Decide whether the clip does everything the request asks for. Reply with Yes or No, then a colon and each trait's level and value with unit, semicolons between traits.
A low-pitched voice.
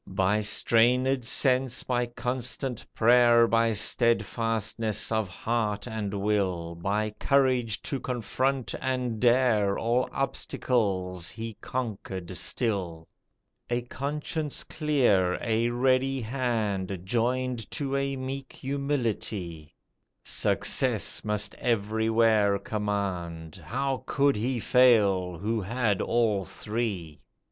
Yes: low, 115 Hz